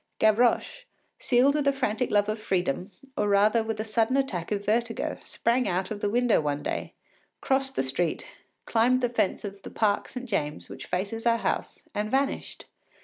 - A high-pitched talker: Yes, high, 220 Hz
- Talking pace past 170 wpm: Yes, average, 185 wpm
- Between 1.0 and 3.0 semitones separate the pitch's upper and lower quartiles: No, average, 3.5 semitones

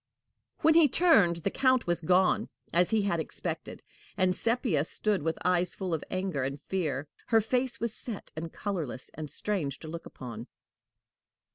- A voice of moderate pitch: Yes, medium, 180 Hz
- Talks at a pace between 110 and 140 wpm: No, average, 165 wpm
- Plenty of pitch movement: Yes, wide, 5.8 semitones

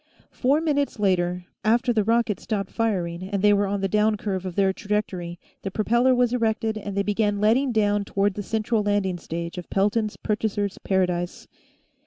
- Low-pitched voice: No, high, 205 Hz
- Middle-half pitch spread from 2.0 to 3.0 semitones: Yes, narrow, 2.6 semitones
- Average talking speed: Yes, average, 180 wpm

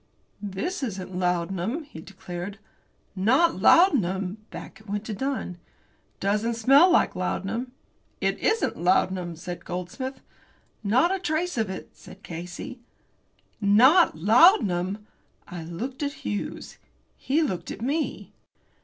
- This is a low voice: No, high, 205 Hz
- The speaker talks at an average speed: No, slow, 125 wpm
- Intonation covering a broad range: Yes, wide, 6.8 semitones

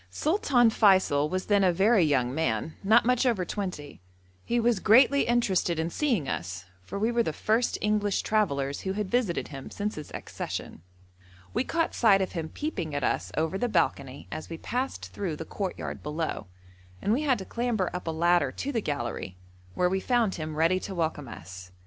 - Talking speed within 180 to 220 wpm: Yes, average, 190 wpm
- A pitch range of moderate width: No, wide, 6.7 semitones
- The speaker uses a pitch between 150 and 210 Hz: Yes, high, 190 Hz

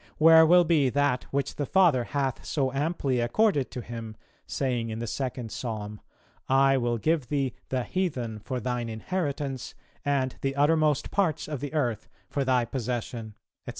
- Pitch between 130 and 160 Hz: Yes, low, 135 Hz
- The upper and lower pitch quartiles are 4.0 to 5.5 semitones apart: No, average, 3.5 semitones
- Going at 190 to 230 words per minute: No, average, 165 wpm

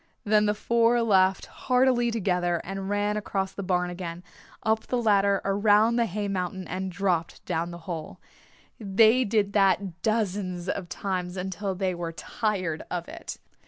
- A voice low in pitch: No, high, 195 Hz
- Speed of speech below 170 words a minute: Yes, average, 160 wpm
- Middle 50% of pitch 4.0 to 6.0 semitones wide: No, average, 2.9 semitones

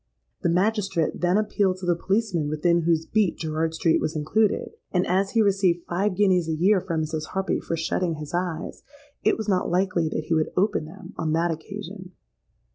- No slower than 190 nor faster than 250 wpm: Yes, average, 195 wpm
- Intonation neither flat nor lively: Yes, average, 3.2 semitones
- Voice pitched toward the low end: No, medium, 175 Hz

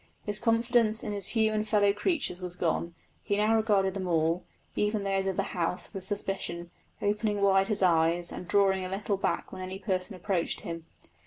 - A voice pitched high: Yes, high, 195 Hz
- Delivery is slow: No, average, 185 wpm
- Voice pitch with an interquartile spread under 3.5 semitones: Yes, narrow, 2.5 semitones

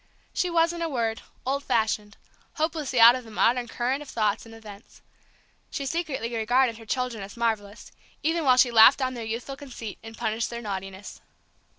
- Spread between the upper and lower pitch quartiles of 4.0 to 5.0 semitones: No, average, 3.4 semitones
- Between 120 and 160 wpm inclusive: No, average, 185 wpm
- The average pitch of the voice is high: Yes, high, 235 Hz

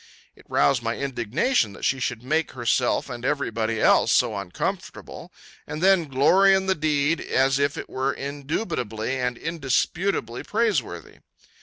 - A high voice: No, medium, 140 Hz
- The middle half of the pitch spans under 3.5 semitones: No, average, 5.0 semitones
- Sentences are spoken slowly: No, average, 150 wpm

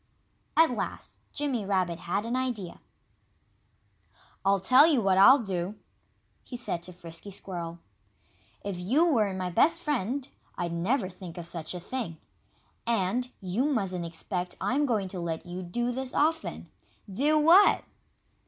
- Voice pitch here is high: Yes, high, 200 Hz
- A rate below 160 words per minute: Yes, average, 150 wpm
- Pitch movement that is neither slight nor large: No, wide, 6.3 semitones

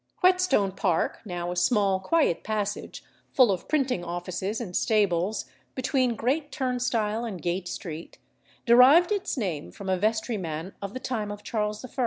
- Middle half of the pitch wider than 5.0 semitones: Yes, wide, 5.5 semitones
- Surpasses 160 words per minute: No, average, 155 wpm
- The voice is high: Yes, high, 210 Hz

